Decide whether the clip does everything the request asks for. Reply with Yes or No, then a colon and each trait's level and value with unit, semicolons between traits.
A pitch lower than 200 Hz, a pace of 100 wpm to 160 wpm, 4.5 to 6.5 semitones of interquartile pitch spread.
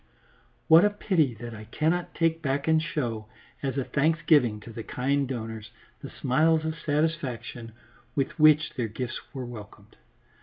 Yes: medium, 140 Hz; average, 155 wpm; average, 5.1 semitones